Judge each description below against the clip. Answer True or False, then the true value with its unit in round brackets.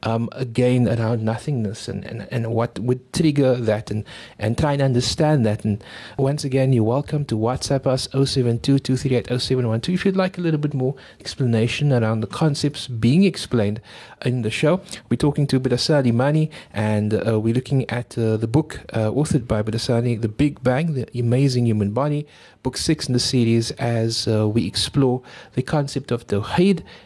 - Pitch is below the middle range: True (125 Hz)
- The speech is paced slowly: False (175 wpm)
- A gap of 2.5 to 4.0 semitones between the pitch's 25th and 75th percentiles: True (3.7 semitones)